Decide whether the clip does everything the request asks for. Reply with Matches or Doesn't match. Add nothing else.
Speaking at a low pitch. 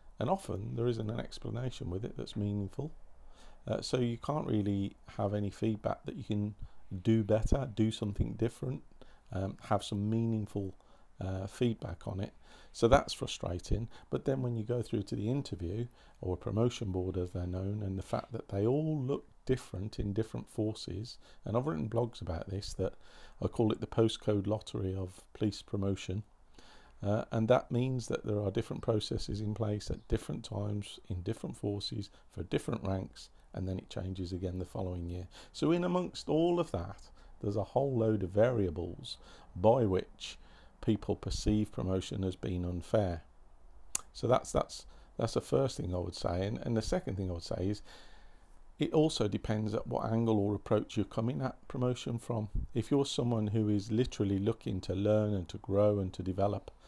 Matches